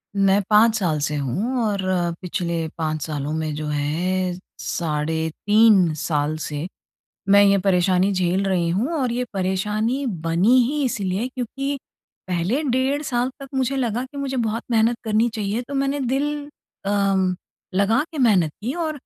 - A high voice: Yes, high, 200 Hz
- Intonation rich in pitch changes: Yes, wide, 6.3 semitones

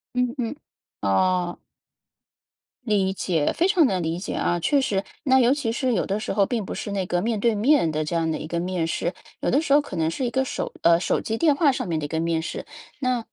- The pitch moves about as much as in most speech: No, wide, 6.9 semitones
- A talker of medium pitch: No, high, 200 Hz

